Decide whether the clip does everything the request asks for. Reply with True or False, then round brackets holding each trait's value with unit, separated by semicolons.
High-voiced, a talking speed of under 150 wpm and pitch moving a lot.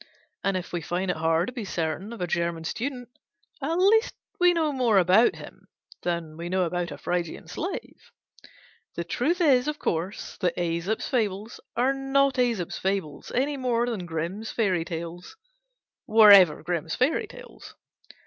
False (195 Hz; 165 wpm; 6.8 semitones)